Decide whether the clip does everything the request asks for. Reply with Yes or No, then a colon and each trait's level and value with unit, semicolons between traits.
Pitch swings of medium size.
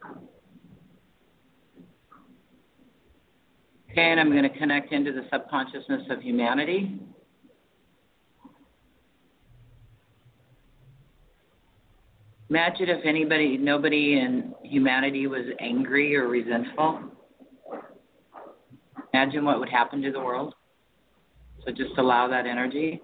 Yes: average, 4.1 semitones